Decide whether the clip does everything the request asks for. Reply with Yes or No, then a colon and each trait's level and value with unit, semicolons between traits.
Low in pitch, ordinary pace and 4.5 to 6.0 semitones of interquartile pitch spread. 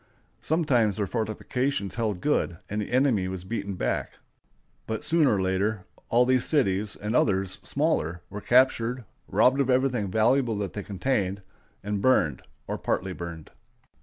Yes: low, 110 Hz; average, 150 wpm; average, 4.9 semitones